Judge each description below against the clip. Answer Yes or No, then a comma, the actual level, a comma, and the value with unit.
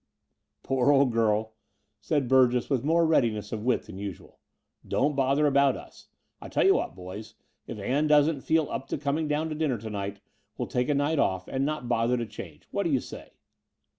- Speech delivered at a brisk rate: Yes, fast, 210 wpm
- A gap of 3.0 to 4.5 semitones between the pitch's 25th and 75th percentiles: No, average, 4.9 semitones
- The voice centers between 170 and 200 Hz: No, low, 130 Hz